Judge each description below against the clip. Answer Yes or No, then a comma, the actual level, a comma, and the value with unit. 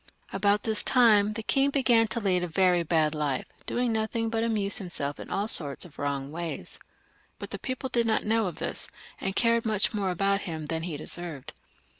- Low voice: No, high, 200 Hz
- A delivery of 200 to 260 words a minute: Yes, fast, 205 wpm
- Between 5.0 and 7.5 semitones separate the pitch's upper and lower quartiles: Yes, average, 5.3 semitones